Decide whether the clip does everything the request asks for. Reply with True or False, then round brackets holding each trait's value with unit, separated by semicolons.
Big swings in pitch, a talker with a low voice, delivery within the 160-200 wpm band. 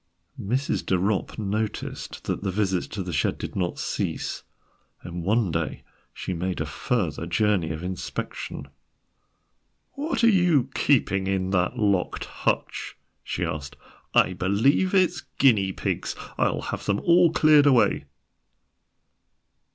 False (6.8 semitones; 100 Hz; 135 wpm)